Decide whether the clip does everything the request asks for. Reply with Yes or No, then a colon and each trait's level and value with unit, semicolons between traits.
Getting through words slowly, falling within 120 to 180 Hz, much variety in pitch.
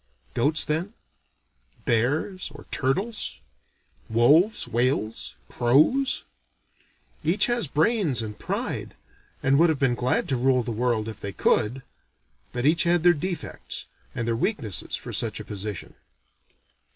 Yes: slow, 130 wpm; low, 135 Hz; wide, 6.6 semitones